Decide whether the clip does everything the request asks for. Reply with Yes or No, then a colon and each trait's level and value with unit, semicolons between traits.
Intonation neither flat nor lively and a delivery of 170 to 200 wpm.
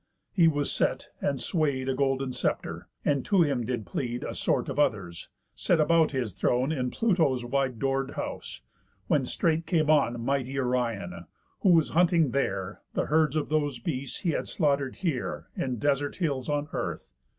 Yes: average, 3.7 semitones; average, 175 wpm